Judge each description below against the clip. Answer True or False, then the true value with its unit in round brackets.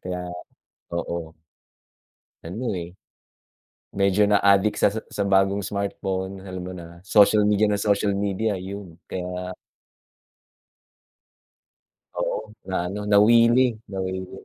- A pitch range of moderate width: False (1.9 semitones)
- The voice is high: False (100 Hz)